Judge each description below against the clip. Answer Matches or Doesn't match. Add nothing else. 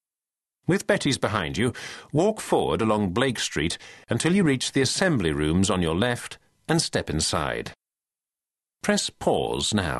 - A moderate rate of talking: Matches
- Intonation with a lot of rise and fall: Matches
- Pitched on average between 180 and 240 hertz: Doesn't match